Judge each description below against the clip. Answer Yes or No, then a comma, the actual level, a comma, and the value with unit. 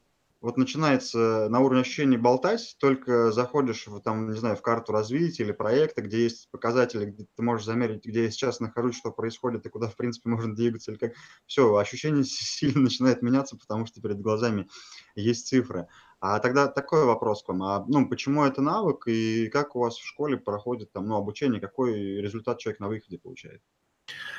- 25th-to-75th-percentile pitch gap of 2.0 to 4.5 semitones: Yes, average, 2.8 semitones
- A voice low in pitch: Yes, low, 115 Hz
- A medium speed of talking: No, fast, 185 wpm